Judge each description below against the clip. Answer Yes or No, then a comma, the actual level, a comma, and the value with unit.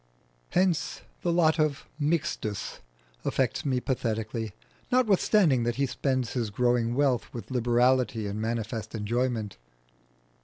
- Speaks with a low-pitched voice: Yes, low, 125 Hz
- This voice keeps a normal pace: No, slow, 115 wpm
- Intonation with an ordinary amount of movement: Yes, average, 4.3 semitones